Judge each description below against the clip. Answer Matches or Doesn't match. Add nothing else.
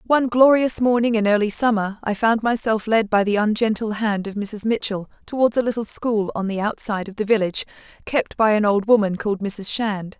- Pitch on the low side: Doesn't match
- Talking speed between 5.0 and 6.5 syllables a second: Matches